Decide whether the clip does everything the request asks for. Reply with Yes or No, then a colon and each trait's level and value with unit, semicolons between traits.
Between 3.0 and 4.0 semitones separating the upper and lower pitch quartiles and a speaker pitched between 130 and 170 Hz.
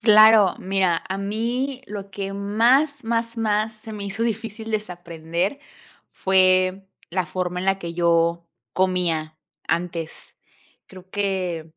No: average, 3.6 semitones; high, 195 Hz